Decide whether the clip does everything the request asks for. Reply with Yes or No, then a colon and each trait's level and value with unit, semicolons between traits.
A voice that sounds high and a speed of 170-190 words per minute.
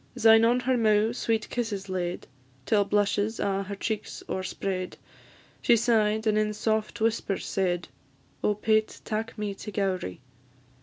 No: high, 210 Hz; average, 145 wpm